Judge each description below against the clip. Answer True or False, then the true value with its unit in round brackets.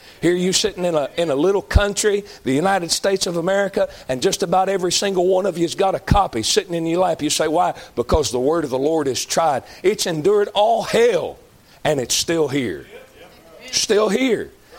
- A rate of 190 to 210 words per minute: True (205 wpm)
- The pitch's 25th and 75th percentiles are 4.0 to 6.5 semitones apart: False (3.3 semitones)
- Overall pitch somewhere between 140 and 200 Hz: True (185 Hz)